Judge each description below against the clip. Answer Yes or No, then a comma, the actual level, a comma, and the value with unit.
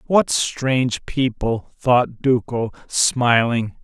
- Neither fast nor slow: No, slow, 95 wpm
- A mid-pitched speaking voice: No, low, 125 Hz